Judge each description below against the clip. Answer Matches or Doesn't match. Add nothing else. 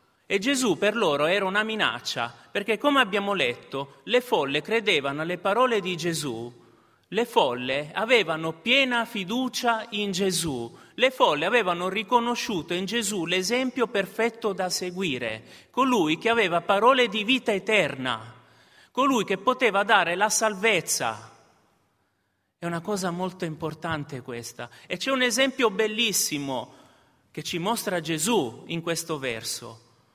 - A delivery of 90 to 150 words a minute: Matches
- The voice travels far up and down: Matches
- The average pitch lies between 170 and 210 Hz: Matches